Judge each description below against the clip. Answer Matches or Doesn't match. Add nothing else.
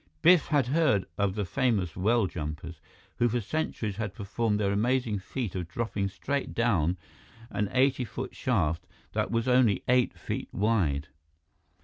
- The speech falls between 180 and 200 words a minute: Doesn't match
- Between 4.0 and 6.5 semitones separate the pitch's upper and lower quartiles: Matches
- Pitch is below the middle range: Matches